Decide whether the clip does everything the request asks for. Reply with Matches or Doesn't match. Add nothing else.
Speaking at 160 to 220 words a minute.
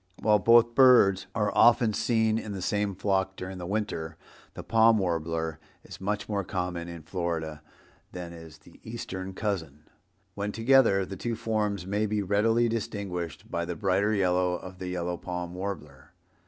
Matches